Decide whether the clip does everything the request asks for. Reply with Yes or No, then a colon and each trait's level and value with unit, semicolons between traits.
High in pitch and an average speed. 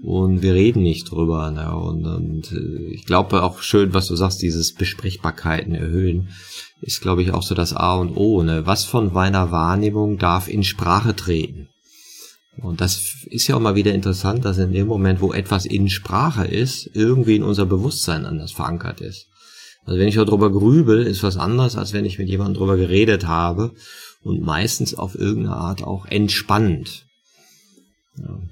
No: very low, 95 Hz; average, 180 wpm